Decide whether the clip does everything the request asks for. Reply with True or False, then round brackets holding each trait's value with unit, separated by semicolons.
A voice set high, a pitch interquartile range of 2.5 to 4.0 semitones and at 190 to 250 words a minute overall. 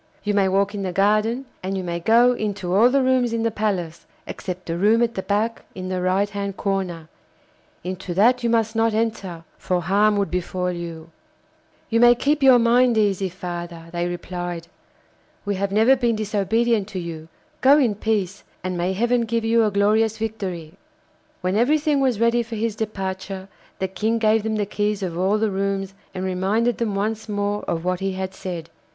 True (205 Hz; 3.4 semitones; 195 wpm)